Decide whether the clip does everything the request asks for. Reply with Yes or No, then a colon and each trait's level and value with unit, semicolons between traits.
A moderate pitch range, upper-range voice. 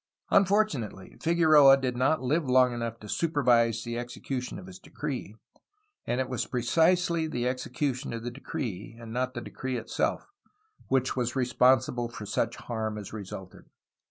No: average, 3.7 semitones; low, 125 Hz